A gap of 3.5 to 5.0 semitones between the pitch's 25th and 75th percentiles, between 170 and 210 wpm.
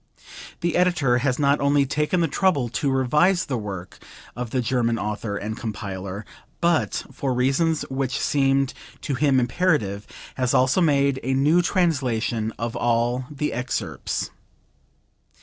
No: average, 4.0 semitones; average, 140 wpm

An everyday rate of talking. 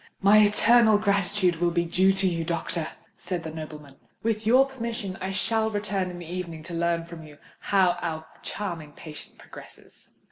Yes: average, 175 wpm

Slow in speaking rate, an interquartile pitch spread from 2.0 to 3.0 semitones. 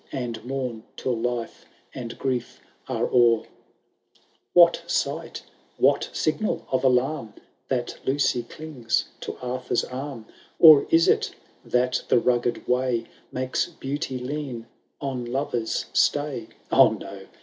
Yes: slow, 125 wpm; narrow, 2.5 semitones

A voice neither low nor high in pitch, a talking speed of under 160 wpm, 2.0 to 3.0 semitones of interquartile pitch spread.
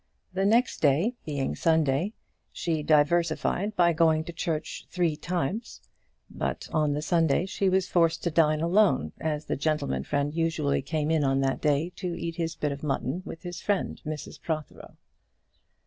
No: medium, 160 Hz; average, 165 wpm; average, 2.7 semitones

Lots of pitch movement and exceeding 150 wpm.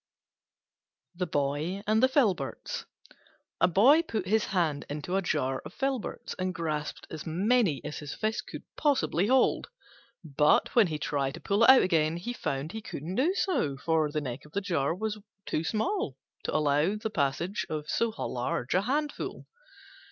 Yes: wide, 6.6 semitones; average, 175 wpm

